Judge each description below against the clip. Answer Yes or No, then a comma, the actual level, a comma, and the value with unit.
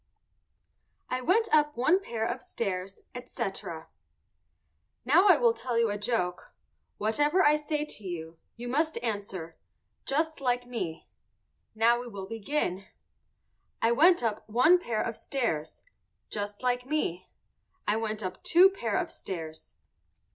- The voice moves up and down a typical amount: No, wide, 6.7 semitones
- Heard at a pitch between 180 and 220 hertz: No, high, 235 Hz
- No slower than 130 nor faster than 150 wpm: Yes, average, 140 wpm